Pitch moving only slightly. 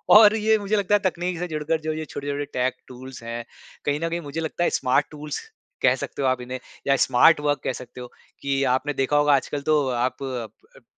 No: average, 4.2 semitones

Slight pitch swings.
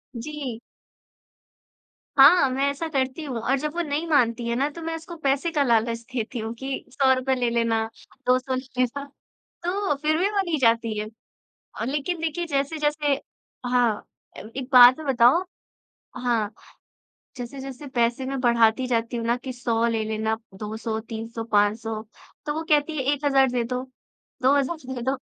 No: average, 3.8 semitones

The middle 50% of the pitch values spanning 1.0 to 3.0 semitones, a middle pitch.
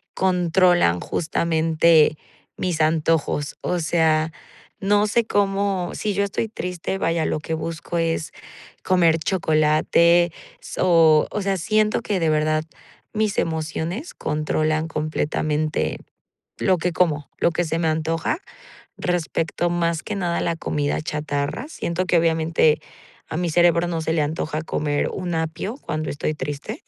Yes: narrow, 2.5 semitones; medium, 165 Hz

